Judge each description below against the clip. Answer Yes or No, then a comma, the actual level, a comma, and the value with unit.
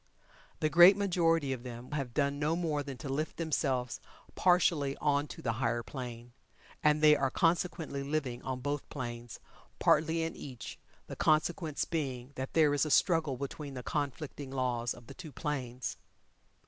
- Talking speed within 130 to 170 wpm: Yes, average, 165 wpm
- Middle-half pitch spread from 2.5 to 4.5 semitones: Yes, average, 3.5 semitones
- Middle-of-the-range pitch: Yes, medium, 145 Hz